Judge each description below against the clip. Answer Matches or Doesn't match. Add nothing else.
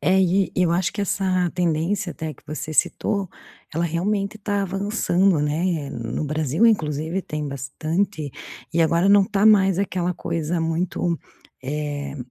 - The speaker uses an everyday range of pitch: Matches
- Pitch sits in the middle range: Matches